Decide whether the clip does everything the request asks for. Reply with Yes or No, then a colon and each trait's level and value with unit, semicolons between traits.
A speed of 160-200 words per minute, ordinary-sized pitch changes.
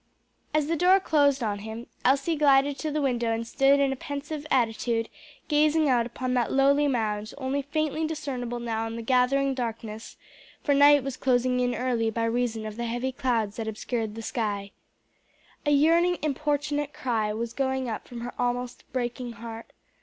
Yes: average, 175 wpm; average, 3.8 semitones